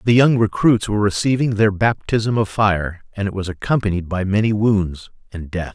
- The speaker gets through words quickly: No, average, 190 wpm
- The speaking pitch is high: No, low, 100 Hz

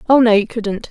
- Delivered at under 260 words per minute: No, fast, 265 wpm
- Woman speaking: Yes, female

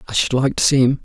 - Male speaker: Yes, male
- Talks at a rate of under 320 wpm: No, fast, 345 wpm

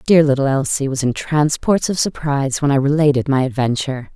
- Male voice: No, female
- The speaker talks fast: No, average, 190 wpm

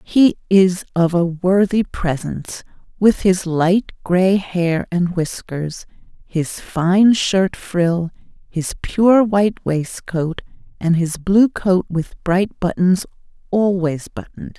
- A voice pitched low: No, medium, 180 Hz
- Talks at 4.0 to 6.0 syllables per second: No, 3.3 syllables/s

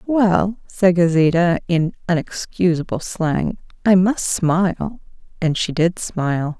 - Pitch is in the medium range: Yes, medium, 175 Hz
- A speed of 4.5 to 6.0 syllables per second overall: No, 3.8 syllables/s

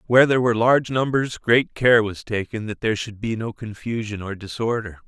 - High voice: No, low, 115 Hz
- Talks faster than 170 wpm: Yes, average, 200 wpm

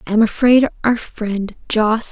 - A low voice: No, high, 225 Hz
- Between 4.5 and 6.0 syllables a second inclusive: No, 4.2 syllables/s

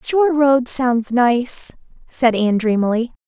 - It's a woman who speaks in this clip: Yes, female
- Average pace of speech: No, slow, 130 wpm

